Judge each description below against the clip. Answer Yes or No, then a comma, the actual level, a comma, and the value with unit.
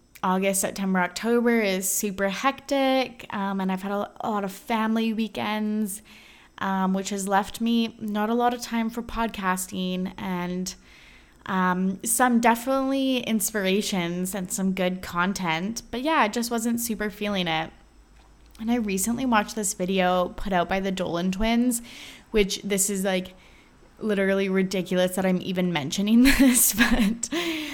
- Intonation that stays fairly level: No, average, 3.6 semitones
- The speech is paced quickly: No, average, 145 wpm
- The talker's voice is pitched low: No, high, 205 Hz